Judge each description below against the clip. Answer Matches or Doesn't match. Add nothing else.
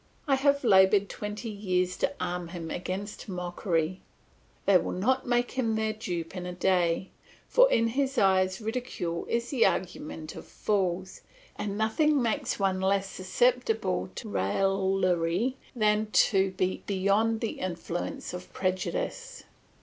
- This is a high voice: Matches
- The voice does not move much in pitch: Doesn't match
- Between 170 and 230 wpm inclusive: Doesn't match